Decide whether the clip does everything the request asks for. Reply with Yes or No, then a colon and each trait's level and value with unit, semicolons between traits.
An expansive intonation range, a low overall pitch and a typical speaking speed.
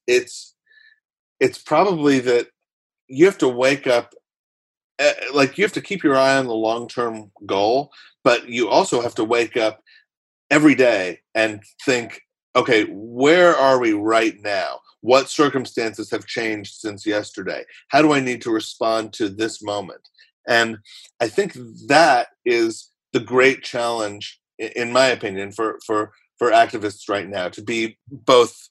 Yes: wide, 7.5 semitones; low, 120 Hz; average, 155 wpm